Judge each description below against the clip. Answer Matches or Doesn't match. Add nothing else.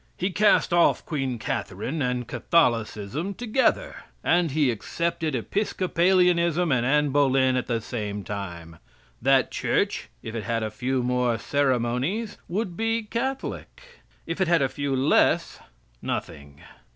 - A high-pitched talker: Doesn't match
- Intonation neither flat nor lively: Doesn't match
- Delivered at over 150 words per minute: Doesn't match